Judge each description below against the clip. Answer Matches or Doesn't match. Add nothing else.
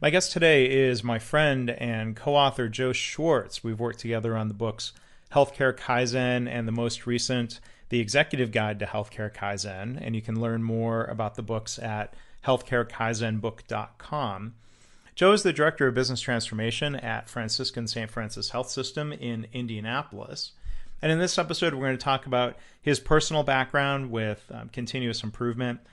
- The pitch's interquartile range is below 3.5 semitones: Matches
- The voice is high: Doesn't match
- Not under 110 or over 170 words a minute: Matches